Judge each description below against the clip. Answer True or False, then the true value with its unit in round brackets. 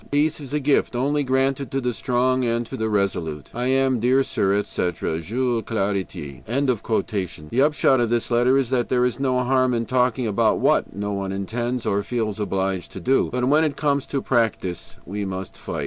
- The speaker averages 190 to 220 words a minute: True (195 wpm)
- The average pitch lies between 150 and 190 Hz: False (120 Hz)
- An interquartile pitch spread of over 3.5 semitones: True (4.5 semitones)